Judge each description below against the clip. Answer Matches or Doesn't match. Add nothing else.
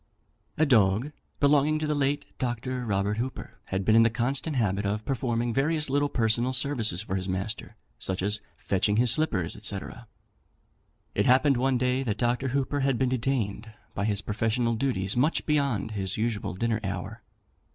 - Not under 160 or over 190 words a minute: Matches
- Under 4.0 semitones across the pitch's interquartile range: Doesn't match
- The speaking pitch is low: Matches